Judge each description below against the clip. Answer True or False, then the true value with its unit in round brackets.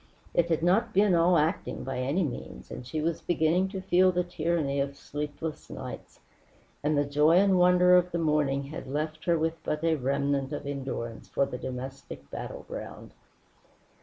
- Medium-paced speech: True (175 wpm)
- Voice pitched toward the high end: False (155 Hz)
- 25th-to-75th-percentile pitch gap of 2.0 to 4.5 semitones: True (4.0 semitones)